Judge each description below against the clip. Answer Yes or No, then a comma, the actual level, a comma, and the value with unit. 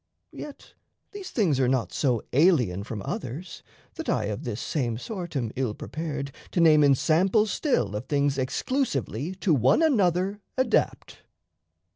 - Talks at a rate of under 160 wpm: Yes, average, 145 wpm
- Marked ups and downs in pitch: Yes, wide, 7.3 semitones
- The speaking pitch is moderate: Yes, medium, 145 Hz